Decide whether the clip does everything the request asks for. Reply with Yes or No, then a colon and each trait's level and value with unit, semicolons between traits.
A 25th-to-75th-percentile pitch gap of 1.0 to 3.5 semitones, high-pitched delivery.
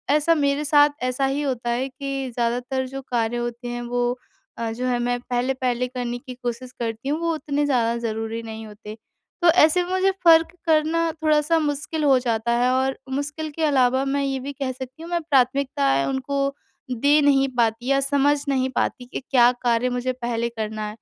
Yes: average, 3.2 semitones; very high, 260 Hz